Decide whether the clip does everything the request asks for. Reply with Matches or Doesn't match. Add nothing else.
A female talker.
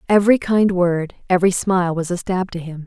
Matches